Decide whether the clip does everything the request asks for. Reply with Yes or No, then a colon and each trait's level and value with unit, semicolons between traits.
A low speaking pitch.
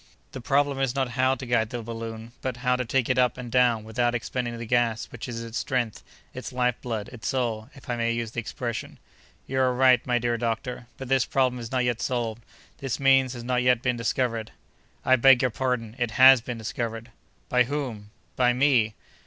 Yes: low, 125 Hz